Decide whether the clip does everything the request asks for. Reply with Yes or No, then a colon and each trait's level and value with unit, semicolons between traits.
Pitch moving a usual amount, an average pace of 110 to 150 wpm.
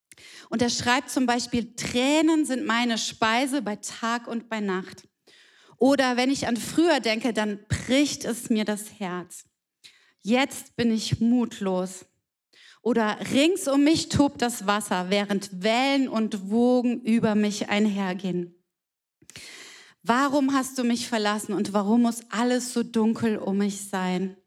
Yes: average, 3.3 semitones; average, 140 wpm